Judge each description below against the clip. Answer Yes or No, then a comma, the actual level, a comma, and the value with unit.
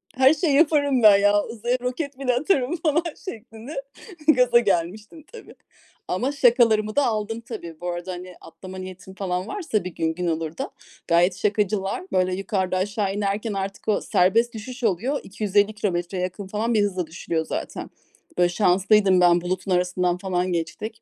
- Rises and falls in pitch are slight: No, average, 4.6 semitones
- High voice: Yes, high, 205 Hz